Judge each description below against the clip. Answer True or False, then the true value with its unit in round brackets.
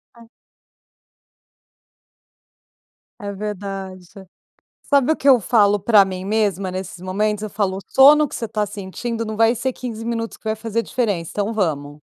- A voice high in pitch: True (210 Hz)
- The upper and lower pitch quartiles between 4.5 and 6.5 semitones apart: False (3.0 semitones)